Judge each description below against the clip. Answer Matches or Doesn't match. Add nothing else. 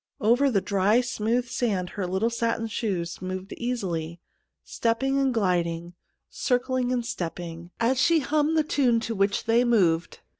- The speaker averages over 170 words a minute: Doesn't match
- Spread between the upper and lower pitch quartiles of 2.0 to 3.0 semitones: Doesn't match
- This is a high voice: Matches